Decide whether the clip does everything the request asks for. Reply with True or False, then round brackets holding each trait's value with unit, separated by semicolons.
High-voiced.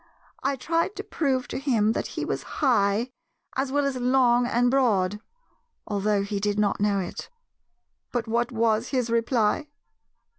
True (240 Hz)